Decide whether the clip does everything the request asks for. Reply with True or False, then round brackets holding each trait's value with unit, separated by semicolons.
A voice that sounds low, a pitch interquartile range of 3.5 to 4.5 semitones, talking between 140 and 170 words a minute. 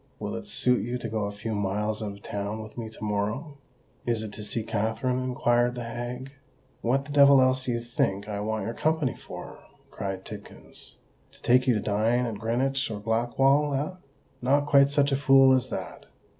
False (120 Hz; 3.8 semitones; 200 wpm)